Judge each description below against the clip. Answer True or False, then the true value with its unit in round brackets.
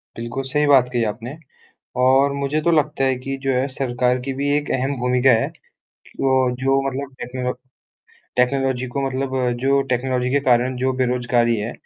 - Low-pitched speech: True (130 Hz)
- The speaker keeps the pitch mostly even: True (1.5 semitones)